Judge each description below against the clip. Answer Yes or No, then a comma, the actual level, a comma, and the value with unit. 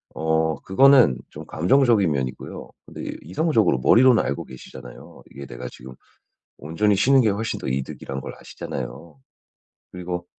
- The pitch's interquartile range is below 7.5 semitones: No, wide, 8.5 semitones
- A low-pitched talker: Yes, very low, 85 Hz